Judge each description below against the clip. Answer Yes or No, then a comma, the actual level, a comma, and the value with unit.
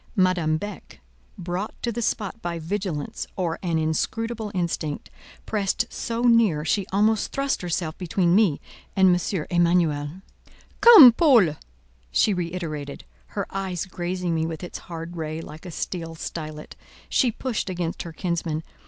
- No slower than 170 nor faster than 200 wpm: No, average, 145 wpm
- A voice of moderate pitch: Yes, medium, 180 Hz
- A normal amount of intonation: Yes, average, 4.1 semitones